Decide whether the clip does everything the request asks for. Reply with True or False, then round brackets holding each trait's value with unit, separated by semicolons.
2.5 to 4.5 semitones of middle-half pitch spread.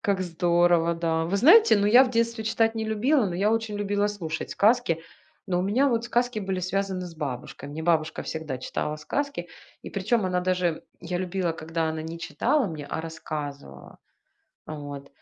False (5.0 semitones)